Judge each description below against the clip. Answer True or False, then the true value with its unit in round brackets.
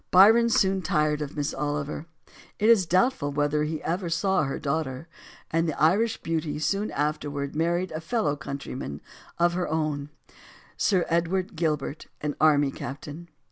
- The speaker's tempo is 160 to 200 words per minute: False (150 wpm)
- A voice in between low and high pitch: True (155 Hz)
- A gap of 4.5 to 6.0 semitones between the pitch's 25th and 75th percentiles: False (3.7 semitones)